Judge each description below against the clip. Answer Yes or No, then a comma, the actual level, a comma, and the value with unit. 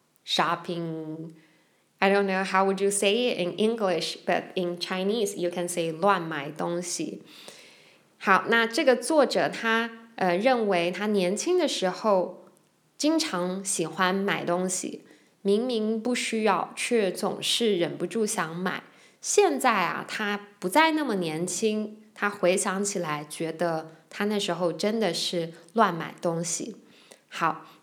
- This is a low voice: No, high, 190 Hz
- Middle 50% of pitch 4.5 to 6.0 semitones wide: No, average, 3.8 semitones